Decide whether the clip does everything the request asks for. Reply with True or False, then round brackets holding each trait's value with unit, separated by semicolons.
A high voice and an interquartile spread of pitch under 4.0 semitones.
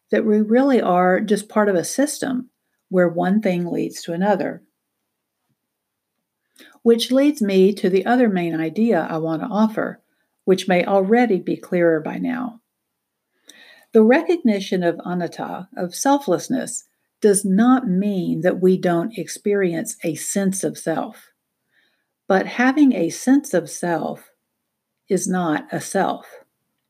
False (200 Hz; 5.1 semitones)